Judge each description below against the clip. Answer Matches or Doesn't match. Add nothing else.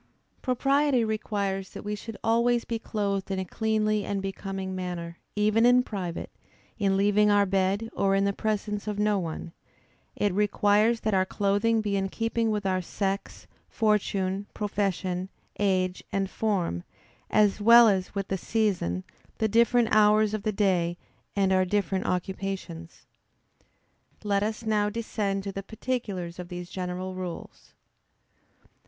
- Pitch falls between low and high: Doesn't match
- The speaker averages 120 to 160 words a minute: Matches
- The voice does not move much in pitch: Matches